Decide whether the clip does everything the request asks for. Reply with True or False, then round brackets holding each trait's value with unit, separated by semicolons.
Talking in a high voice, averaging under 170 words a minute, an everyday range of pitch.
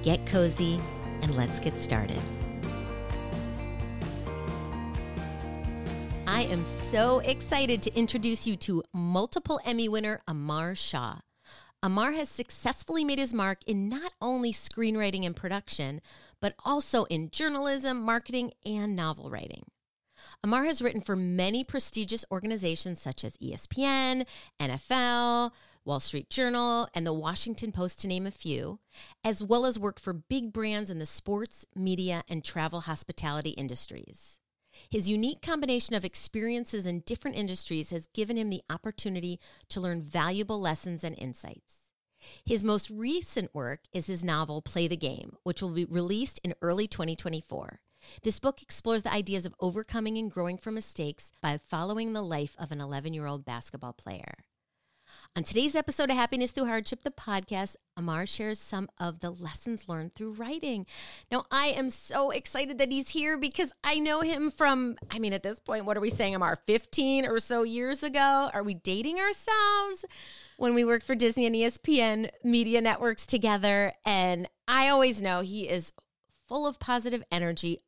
False (210 Hz; 155 wpm; 6.2 semitones)